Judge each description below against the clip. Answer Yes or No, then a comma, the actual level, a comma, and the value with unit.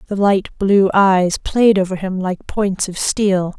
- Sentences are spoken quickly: No, average, 185 wpm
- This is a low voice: No, high, 195 Hz